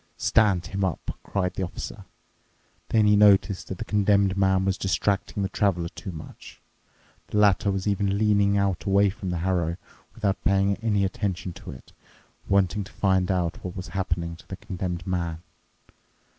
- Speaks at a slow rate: No, average, 170 wpm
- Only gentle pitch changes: Yes, narrow, 1.8 semitones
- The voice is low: Yes, very low, 95 Hz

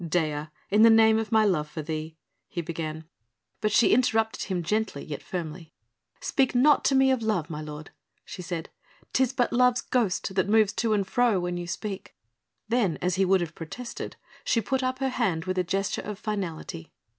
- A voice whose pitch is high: Yes, high, 195 Hz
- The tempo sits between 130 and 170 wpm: No, average, 200 wpm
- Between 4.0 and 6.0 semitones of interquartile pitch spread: Yes, average, 5.2 semitones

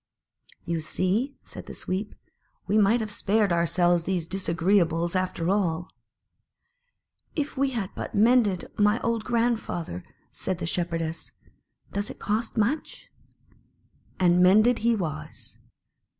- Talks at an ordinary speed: No, slow, 125 wpm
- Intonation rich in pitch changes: No, average, 4.4 semitones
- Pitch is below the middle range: No, high, 195 Hz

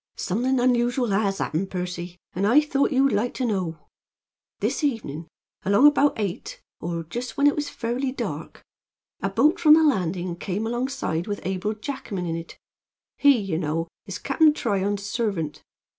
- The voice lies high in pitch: Yes, high, 210 Hz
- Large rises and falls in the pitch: Yes, wide, 6.5 semitones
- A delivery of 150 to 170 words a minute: Yes, average, 160 wpm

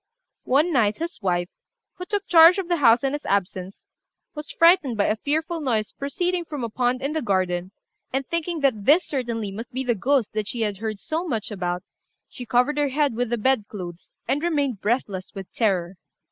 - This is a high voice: Yes, high, 245 Hz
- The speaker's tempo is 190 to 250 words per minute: Yes, average, 200 wpm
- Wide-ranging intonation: Yes, wide, 6.3 semitones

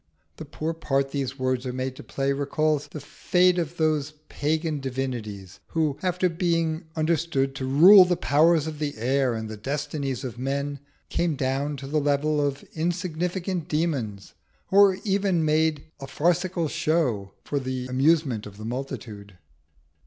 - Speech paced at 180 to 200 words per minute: No, average, 160 wpm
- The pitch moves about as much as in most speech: Yes, average, 3.9 semitones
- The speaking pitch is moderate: Yes, medium, 145 Hz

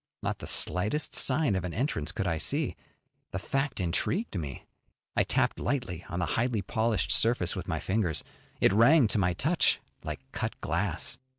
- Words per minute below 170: No, average, 175 wpm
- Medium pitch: No, low, 100 Hz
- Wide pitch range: Yes, wide, 6.4 semitones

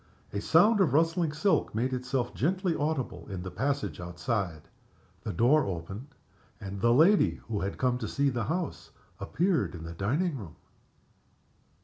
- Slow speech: No, average, 155 wpm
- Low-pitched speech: Yes, low, 125 Hz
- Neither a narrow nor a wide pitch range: No, wide, 8.3 semitones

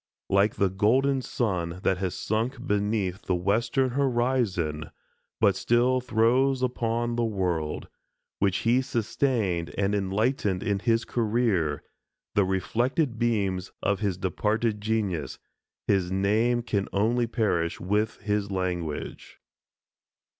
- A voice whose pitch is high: No, low, 105 Hz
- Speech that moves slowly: Yes, slow, 120 wpm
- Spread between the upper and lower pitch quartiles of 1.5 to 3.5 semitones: No, average, 3.9 semitones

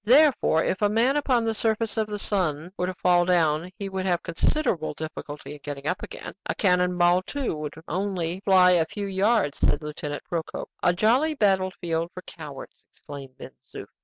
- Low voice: No, medium, 180 Hz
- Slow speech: No, average, 190 wpm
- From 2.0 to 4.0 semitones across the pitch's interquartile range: No, average, 4.4 semitones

